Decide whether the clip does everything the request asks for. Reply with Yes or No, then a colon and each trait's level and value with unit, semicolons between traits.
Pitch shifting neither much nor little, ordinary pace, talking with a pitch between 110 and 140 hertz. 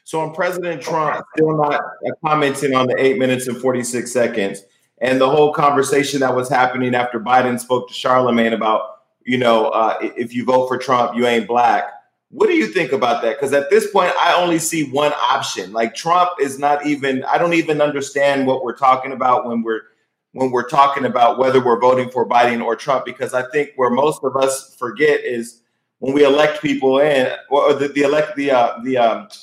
No: average, 3.0 semitones; fast, 210 wpm; low, 130 Hz